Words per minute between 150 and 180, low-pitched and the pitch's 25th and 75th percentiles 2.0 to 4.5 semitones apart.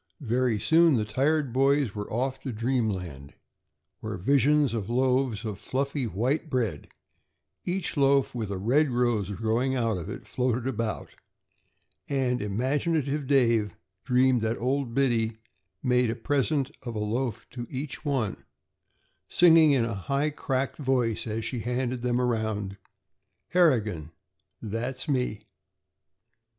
No: slow, 135 wpm; low, 125 Hz; average, 3.7 semitones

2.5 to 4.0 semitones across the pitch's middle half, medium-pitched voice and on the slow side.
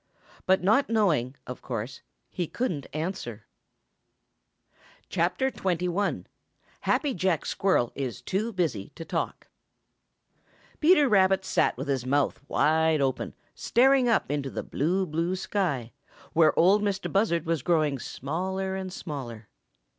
No: average, 5.3 semitones; medium, 175 Hz; slow, 125 wpm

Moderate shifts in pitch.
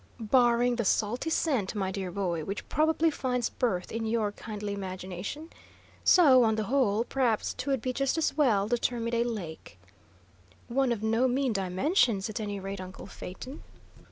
Yes: average, 4.4 semitones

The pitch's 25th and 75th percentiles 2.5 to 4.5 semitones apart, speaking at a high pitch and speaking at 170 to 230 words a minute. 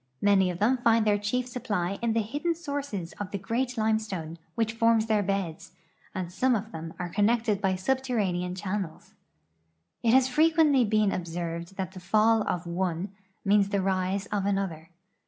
Yes: average, 3.8 semitones; high, 205 Hz; average, 175 wpm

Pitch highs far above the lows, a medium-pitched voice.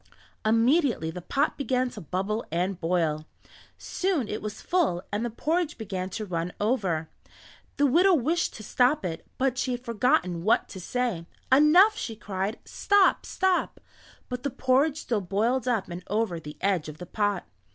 No: wide, 6.4 semitones; high, 220 Hz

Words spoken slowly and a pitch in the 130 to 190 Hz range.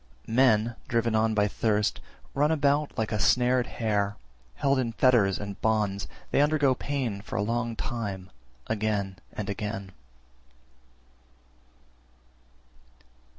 No: slow, 120 wpm; low, 110 Hz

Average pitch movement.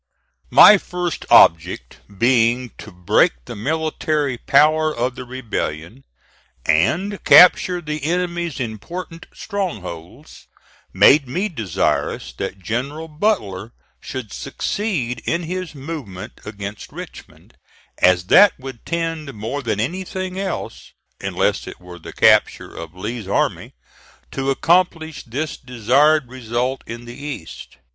No: wide, 6.8 semitones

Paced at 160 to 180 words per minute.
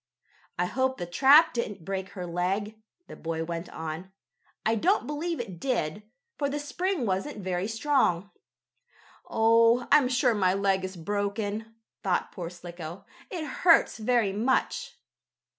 No: average, 140 wpm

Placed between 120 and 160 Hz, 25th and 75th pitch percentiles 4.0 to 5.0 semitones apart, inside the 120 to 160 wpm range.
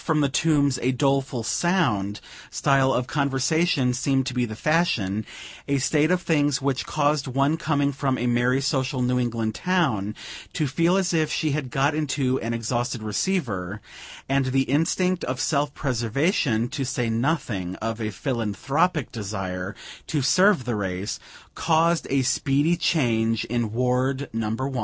Yes: low, 135 Hz; average, 4.4 semitones; average, 155 wpm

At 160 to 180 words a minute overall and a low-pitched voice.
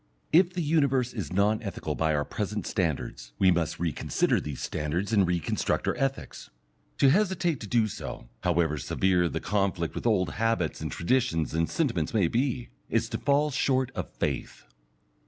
Yes: average, 170 wpm; low, 100 Hz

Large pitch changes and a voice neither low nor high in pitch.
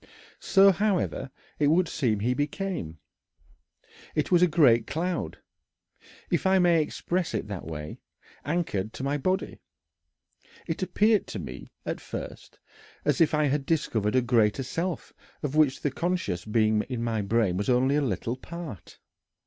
Yes: wide, 7.4 semitones; medium, 145 Hz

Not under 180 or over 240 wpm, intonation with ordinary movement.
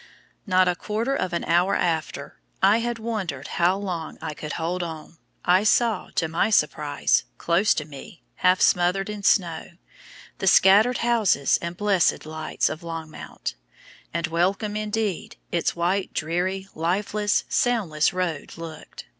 No: average, 145 wpm; average, 4.0 semitones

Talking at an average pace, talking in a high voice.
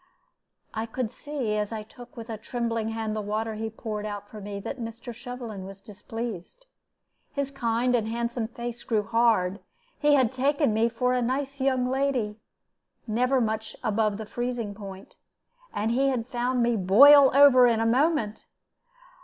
Yes: average, 170 wpm; high, 230 Hz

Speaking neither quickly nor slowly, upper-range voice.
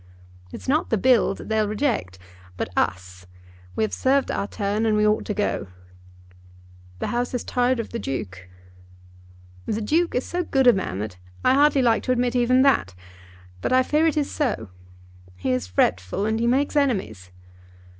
Yes: average, 180 wpm; high, 225 Hz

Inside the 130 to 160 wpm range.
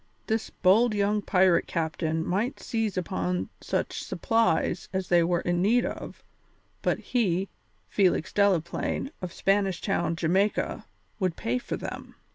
Yes: slow, 135 wpm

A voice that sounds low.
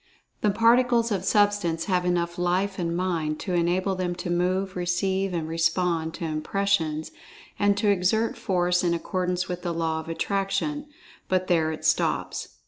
No: medium, 180 Hz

